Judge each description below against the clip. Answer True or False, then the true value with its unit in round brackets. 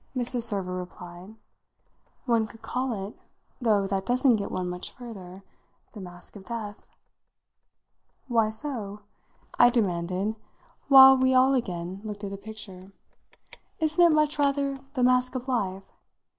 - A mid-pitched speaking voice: False (220 Hz)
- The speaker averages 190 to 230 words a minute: False (140 wpm)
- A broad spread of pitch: False (4.7 semitones)